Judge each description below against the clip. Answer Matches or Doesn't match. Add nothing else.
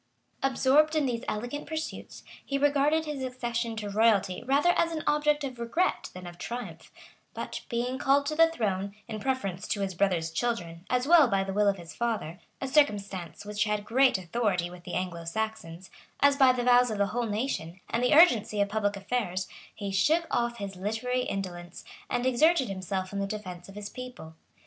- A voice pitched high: Matches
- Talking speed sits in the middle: Matches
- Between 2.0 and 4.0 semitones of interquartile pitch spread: Doesn't match